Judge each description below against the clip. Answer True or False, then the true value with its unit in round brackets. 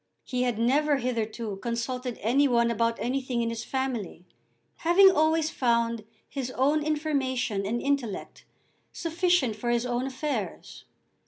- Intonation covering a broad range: False (3.4 semitones)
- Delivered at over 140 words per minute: False (135 wpm)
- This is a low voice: False (250 Hz)